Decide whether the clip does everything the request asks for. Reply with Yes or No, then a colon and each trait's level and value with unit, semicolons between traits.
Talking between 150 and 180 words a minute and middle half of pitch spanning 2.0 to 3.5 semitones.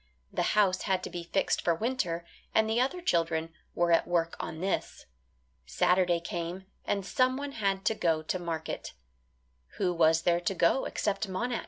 No: average, 170 wpm; average, 3.9 semitones